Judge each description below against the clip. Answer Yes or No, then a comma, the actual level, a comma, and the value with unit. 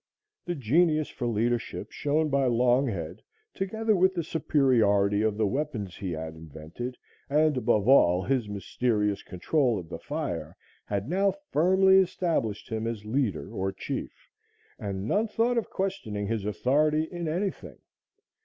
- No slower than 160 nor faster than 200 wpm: No, average, 145 wpm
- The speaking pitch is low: Yes, low, 125 Hz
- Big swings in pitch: Yes, wide, 7.6 semitones